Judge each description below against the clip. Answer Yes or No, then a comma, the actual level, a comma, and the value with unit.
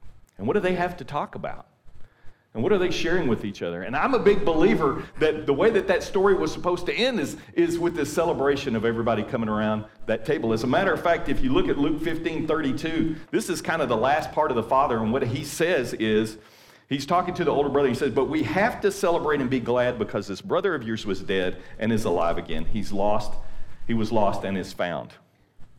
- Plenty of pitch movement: Yes, wide, 7.9 semitones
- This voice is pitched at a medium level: No, low, 130 Hz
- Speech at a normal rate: No, fast, 240 wpm